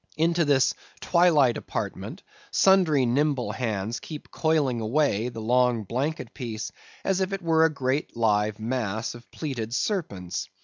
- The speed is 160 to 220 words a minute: No, average, 140 wpm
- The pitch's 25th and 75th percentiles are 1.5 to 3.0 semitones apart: No, wide, 5.6 semitones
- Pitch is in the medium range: No, low, 130 Hz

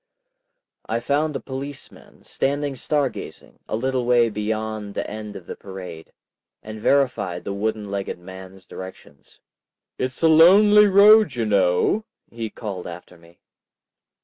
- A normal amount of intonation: No, wide, 6.6 semitones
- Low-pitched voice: Yes, low, 110 Hz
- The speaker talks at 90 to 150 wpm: Yes, average, 140 wpm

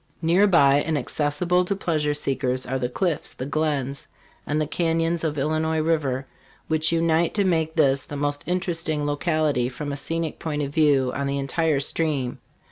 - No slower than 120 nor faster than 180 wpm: Yes, average, 175 wpm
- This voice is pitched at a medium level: Yes, medium, 155 Hz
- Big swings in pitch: No, average, 2.8 semitones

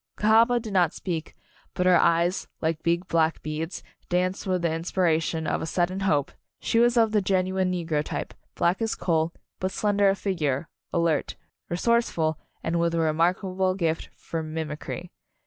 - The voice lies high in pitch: No, medium, 175 Hz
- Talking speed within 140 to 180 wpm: Yes, average, 170 wpm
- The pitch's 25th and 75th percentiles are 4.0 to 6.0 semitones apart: No, average, 2.8 semitones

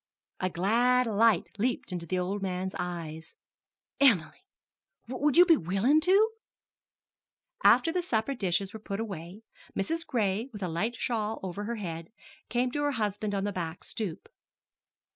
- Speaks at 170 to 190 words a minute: No, average, 155 wpm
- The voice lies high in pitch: Yes, high, 210 Hz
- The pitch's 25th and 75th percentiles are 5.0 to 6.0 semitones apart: Yes, average, 5.3 semitones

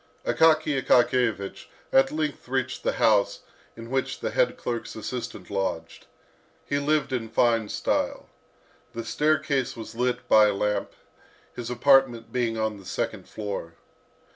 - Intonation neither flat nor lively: Yes, average, 3.5 semitones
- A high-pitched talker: No, low, 120 Hz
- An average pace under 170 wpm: Yes, average, 140 wpm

